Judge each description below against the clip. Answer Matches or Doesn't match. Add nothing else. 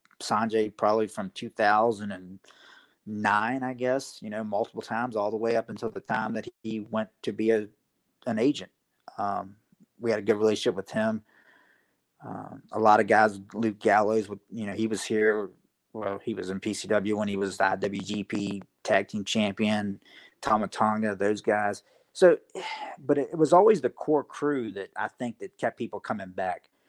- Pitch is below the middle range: Matches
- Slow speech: Doesn't match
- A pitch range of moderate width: Doesn't match